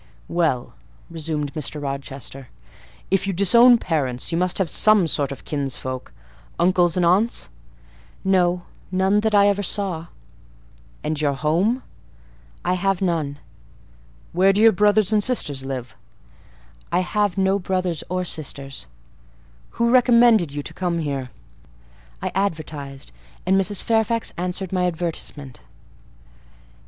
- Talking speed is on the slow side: Yes, slow, 125 wpm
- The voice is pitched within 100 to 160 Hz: No, medium, 180 Hz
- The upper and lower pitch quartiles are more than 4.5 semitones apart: Yes, average, 5.0 semitones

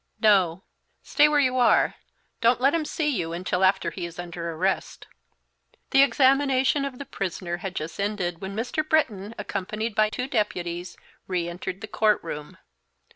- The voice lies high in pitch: Yes, high, 205 Hz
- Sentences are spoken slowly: No, average, 165 wpm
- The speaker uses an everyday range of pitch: No, wide, 6.5 semitones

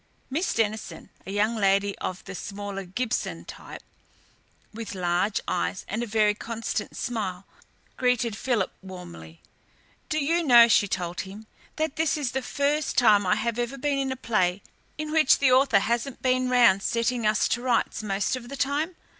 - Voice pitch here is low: No, high, 230 Hz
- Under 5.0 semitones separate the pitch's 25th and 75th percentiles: Yes, average, 4.6 semitones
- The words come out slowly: No, average, 170 wpm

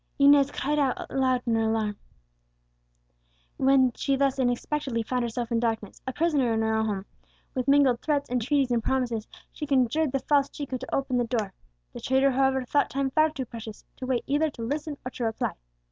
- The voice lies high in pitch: Yes, very high, 260 Hz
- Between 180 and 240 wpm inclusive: Yes, average, 195 wpm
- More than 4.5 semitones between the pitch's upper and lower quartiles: No, average, 3.1 semitones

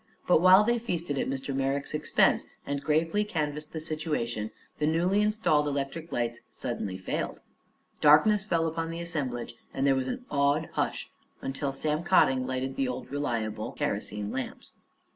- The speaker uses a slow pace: No, average, 160 wpm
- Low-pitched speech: No, medium, 150 Hz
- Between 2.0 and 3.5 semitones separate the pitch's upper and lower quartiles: No, average, 3.9 semitones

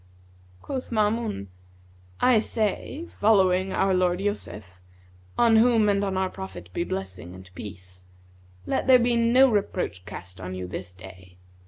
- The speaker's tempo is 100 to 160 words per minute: Yes, average, 145 wpm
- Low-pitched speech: No, medium, 185 Hz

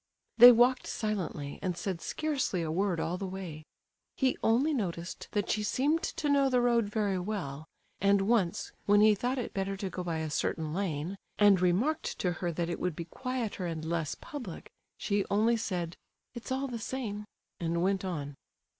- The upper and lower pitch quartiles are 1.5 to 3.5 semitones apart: No, wide, 5.5 semitones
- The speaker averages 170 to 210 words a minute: Yes, average, 185 wpm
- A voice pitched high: Yes, high, 195 Hz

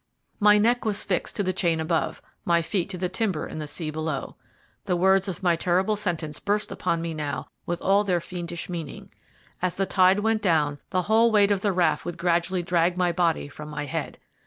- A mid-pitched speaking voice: Yes, medium, 180 Hz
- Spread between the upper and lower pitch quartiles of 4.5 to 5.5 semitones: No, average, 3.0 semitones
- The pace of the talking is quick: Yes, fast, 210 wpm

